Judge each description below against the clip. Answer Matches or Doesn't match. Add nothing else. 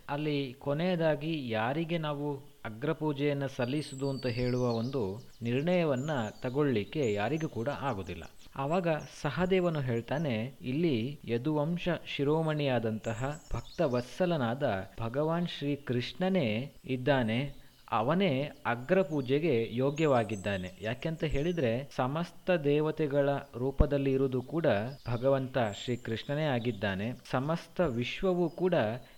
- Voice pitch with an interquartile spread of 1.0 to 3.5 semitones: Doesn't match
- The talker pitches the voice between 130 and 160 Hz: Matches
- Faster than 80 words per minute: Matches